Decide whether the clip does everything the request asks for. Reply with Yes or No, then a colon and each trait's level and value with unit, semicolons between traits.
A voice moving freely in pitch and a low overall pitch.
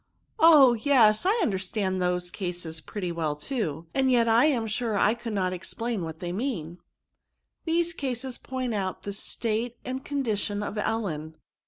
No: wide, 5.8 semitones; high, 215 Hz